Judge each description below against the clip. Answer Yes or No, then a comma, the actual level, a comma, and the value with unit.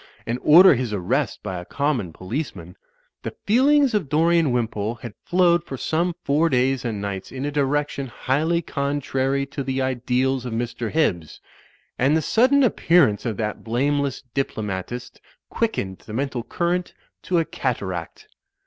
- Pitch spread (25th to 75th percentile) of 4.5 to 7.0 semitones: Yes, wide, 5.4 semitones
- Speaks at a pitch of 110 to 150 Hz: Yes, low, 135 Hz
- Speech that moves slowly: No, average, 155 wpm